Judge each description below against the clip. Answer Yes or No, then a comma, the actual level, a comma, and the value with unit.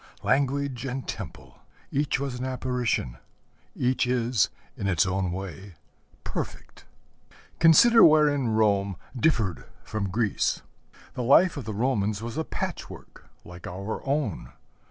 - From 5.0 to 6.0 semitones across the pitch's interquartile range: Yes, wide, 5.6 semitones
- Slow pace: Yes, slow, 125 wpm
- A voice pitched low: Yes, low, 120 Hz